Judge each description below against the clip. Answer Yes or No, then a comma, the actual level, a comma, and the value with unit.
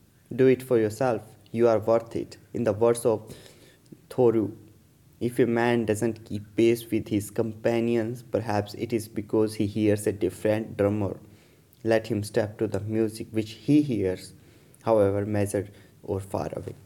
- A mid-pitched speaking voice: No, low, 110 Hz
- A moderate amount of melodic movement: No, narrow, 2.0 semitones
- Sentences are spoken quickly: No, average, 160 wpm